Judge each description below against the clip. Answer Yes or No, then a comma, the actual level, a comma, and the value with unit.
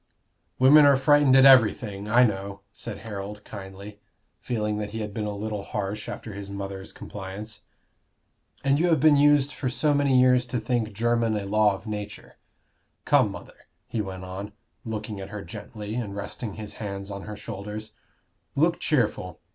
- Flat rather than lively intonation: No, average, 3.7 semitones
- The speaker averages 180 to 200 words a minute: No, average, 170 wpm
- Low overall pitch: Yes, low, 105 Hz